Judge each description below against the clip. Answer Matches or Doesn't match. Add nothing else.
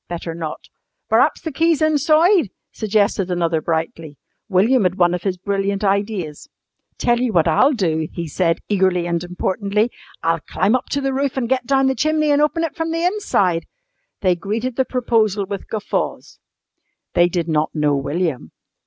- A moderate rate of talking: Matches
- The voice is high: Matches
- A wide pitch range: Matches